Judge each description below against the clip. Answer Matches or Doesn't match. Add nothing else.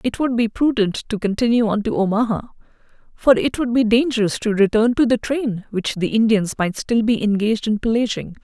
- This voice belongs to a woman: Matches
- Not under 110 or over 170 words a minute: Doesn't match